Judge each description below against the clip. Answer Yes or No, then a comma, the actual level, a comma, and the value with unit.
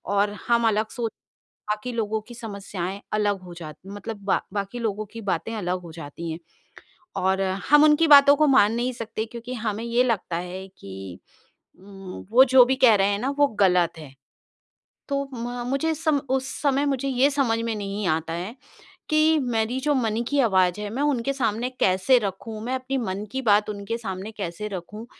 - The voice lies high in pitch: Yes, high, 220 Hz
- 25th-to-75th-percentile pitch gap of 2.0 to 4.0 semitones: No, average, 4.6 semitones